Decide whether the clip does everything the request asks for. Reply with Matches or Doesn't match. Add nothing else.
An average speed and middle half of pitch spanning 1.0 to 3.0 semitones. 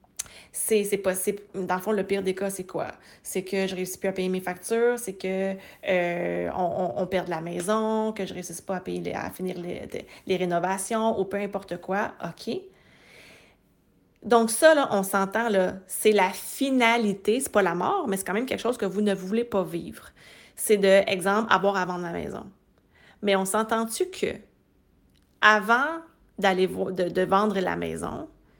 Matches